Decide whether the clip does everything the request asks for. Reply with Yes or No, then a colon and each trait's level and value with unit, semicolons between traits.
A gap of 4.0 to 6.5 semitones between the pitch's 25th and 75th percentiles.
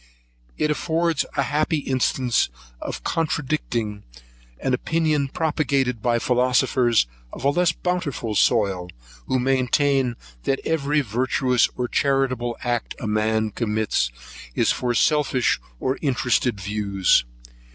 No: average, 3.6 semitones